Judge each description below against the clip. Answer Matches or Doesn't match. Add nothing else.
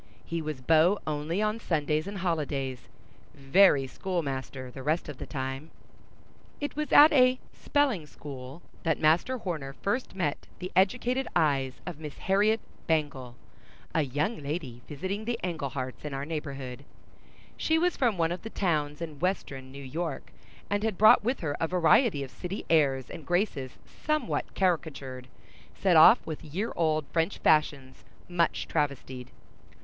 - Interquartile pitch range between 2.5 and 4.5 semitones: Doesn't match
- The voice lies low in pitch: Doesn't match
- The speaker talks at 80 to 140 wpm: Doesn't match